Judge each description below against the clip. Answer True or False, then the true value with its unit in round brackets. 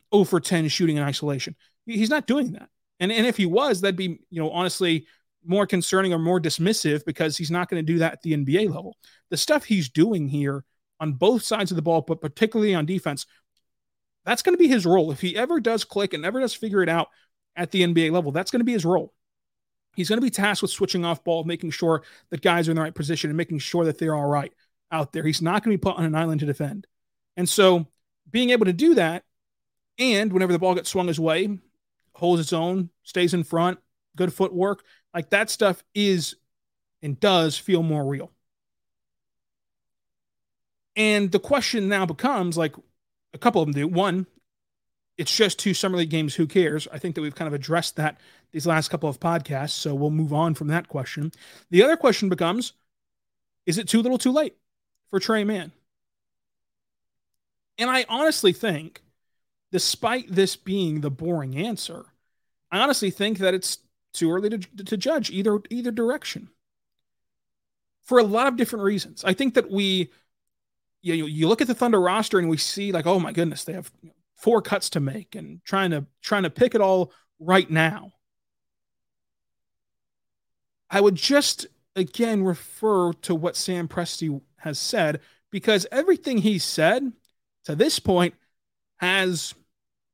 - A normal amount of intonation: True (4.4 semitones)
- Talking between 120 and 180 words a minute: False (190 wpm)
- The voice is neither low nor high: True (180 Hz)